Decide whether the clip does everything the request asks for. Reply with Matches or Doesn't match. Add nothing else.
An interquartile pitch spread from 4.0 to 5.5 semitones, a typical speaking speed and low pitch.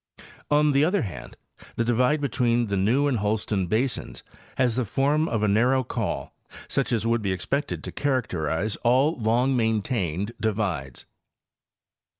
Matches